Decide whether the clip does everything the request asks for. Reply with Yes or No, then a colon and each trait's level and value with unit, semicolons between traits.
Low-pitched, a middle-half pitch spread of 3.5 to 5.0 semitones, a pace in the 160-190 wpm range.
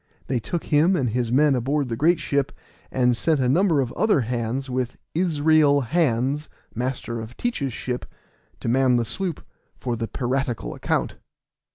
Yes: low, 130 Hz; average, 3.9 semitones; average, 165 wpm